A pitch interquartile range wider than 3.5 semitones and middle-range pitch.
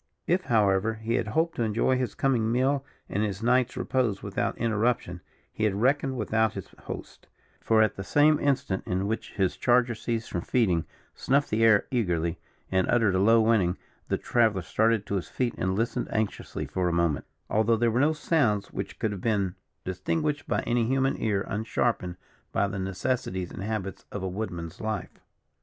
No: average, 3.9 semitones; low, 110 Hz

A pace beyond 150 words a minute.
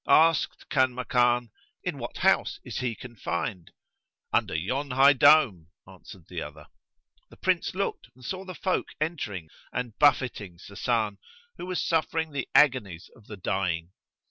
No: average, 145 wpm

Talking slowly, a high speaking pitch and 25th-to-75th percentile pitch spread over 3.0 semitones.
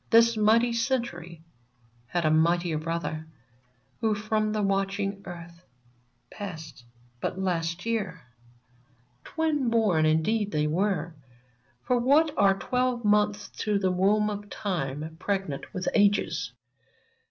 Yes: slow, 120 wpm; high, 195 Hz; average, 4.4 semitones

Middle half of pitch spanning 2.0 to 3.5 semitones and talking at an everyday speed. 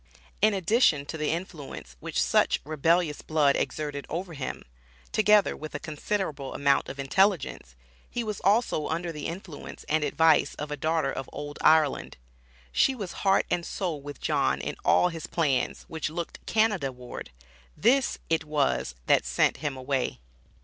No: average, 4.0 semitones; average, 160 wpm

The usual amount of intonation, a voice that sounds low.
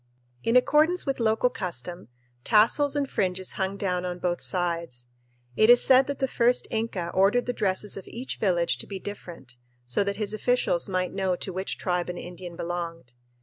No: average, 4.7 semitones; high, 190 Hz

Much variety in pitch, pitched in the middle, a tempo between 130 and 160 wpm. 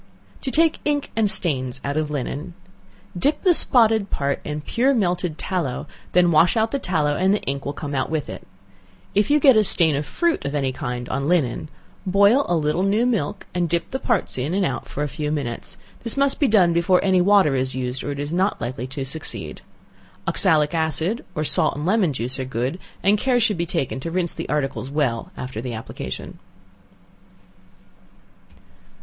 No: wide, 6.4 semitones; medium, 165 Hz; average, 200 wpm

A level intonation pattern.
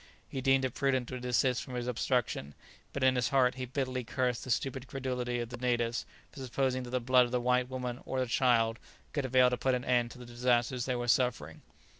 Yes: narrow, 1.1 semitones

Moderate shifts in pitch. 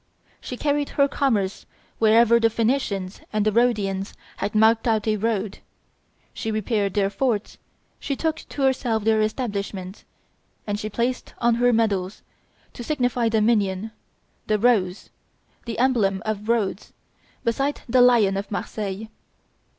Yes: average, 3.0 semitones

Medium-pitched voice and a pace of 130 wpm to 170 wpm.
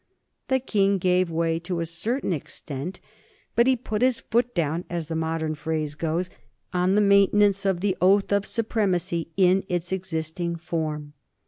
Yes: medium, 180 Hz; average, 160 wpm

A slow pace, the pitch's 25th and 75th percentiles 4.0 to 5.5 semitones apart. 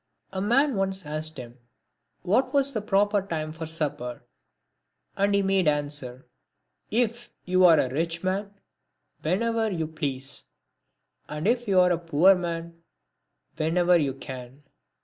No: average, 145 wpm; average, 4.8 semitones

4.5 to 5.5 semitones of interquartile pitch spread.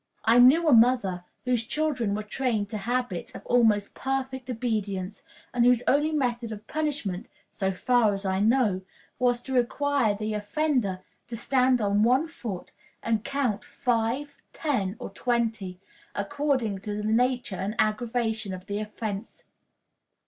No: average, 3.7 semitones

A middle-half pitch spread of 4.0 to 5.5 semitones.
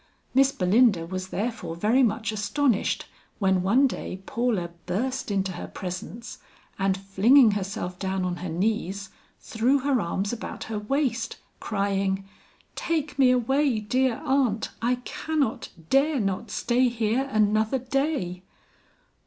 Yes: average, 5.0 semitones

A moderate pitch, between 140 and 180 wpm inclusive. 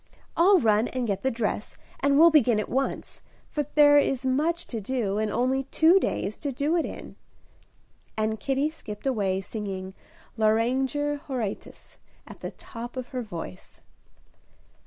No: very high, 255 Hz; average, 155 wpm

